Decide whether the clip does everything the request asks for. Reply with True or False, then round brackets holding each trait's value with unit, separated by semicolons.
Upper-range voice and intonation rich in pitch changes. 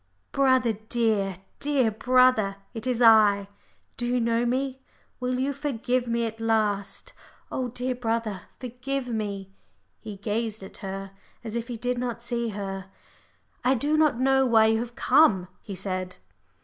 False (235 Hz; 3.2 semitones)